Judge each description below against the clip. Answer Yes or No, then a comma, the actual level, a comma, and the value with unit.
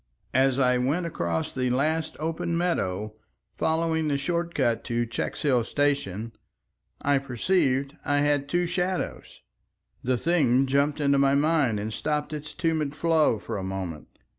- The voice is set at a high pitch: No, medium, 140 Hz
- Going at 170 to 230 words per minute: No, average, 145 wpm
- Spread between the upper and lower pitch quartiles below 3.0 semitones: No, average, 4.3 semitones